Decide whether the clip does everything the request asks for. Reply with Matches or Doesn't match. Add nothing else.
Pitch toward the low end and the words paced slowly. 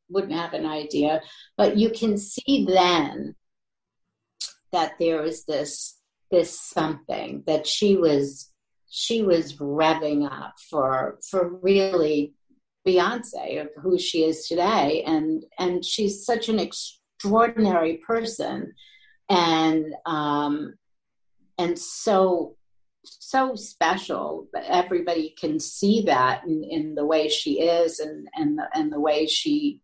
Doesn't match